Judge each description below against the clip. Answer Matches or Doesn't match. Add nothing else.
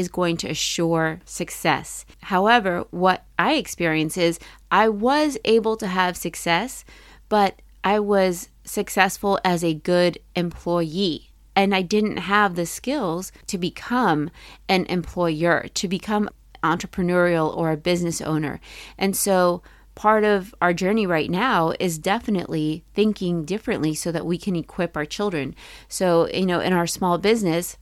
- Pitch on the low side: Doesn't match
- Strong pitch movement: Doesn't match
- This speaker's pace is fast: Doesn't match